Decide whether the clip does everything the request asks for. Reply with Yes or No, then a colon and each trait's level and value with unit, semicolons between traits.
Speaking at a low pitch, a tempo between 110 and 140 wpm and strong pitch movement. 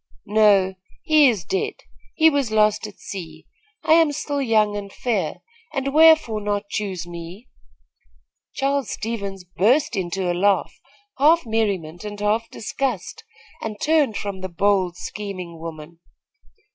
No: high, 210 Hz; slow, 135 wpm; wide, 6.2 semitones